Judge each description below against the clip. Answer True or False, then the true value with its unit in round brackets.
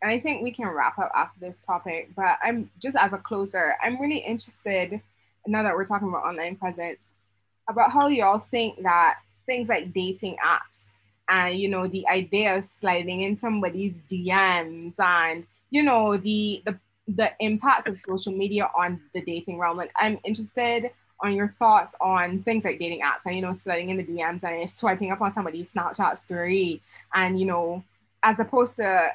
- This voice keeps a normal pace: True (185 wpm)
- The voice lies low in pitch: False (190 Hz)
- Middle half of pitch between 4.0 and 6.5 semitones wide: False (3.6 semitones)